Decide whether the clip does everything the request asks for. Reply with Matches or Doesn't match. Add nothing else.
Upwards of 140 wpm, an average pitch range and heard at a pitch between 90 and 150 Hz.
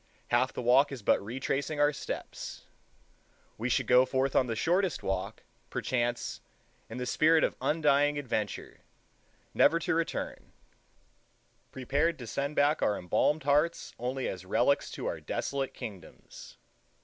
Doesn't match